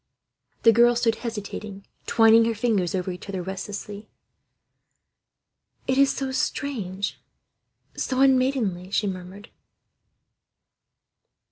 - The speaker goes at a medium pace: No, slow, 100 wpm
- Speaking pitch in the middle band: No, high, 215 Hz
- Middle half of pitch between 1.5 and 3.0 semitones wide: No, average, 3.9 semitones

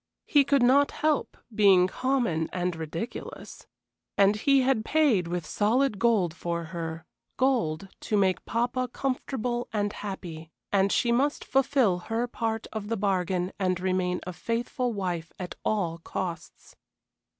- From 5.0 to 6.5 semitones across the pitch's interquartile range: Yes, wide, 5.4 semitones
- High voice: Yes, high, 205 Hz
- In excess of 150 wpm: No, average, 140 wpm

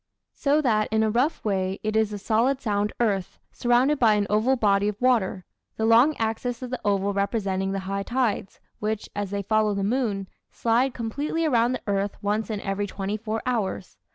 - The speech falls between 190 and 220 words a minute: Yes, average, 195 wpm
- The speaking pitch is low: No, high, 215 Hz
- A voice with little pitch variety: No, average, 3.2 semitones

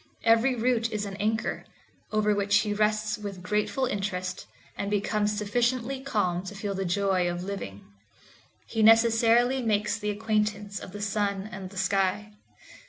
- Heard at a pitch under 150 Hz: No, high, 210 Hz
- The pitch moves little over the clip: Yes, narrow, 2.1 semitones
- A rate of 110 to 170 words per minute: Yes, average, 155 wpm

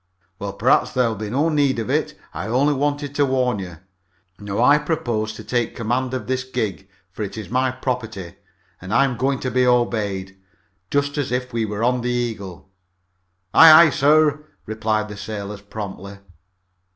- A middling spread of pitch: Yes, average, 4.0 semitones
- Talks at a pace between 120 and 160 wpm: No, average, 175 wpm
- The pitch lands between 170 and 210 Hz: No, low, 120 Hz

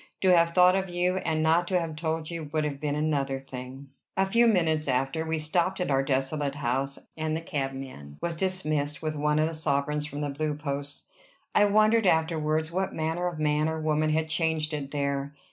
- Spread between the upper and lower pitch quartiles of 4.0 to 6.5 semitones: No, average, 2.7 semitones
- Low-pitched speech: No, medium, 155 Hz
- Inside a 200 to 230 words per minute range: Yes, fast, 205 wpm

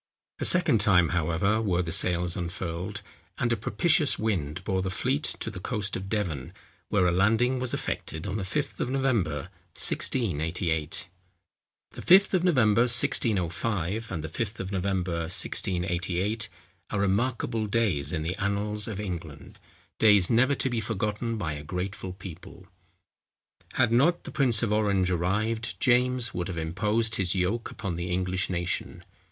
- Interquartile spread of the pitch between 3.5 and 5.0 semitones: Yes, average, 4.5 semitones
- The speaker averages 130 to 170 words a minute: Yes, average, 155 wpm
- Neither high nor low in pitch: No, low, 100 Hz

